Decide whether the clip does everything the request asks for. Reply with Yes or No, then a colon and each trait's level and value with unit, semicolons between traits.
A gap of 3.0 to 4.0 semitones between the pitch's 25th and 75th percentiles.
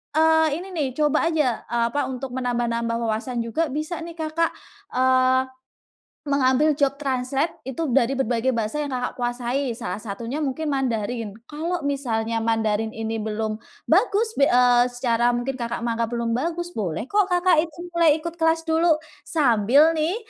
No: average, 5.0 semitones